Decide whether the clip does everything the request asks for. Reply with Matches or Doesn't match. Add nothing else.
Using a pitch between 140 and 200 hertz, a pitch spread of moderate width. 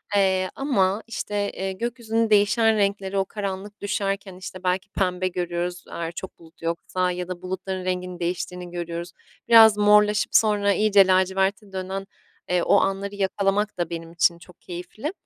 Doesn't match